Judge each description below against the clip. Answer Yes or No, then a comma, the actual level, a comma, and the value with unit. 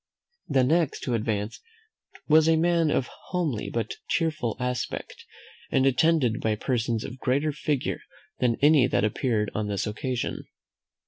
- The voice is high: No, low, 125 Hz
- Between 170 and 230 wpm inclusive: No, average, 145 wpm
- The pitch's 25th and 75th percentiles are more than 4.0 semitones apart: Yes, wide, 5.4 semitones